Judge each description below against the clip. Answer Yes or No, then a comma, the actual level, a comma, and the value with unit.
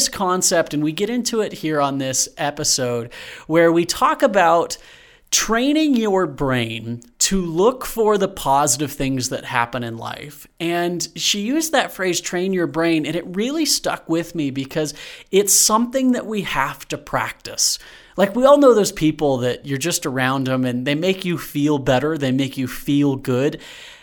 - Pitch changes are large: Yes, wide, 6.8 semitones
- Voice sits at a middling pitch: Yes, medium, 165 Hz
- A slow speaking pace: No, average, 175 wpm